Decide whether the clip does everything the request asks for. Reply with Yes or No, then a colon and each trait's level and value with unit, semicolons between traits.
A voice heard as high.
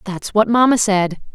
Yes: high, 210 Hz